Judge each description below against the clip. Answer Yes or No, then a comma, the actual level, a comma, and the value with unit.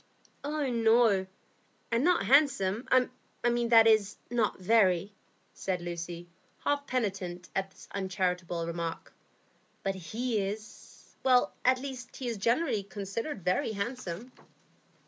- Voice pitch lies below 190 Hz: No, high, 215 Hz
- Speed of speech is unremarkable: No, slow, 105 wpm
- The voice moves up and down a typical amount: Yes, average, 4.8 semitones